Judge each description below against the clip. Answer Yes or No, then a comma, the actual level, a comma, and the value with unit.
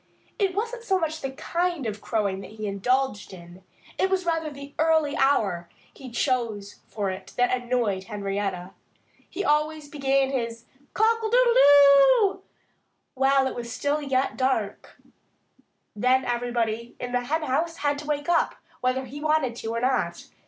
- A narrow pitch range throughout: No, average, 5.3 semitones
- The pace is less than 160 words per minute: Yes, average, 150 wpm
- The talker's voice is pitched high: Yes, very high, 265 Hz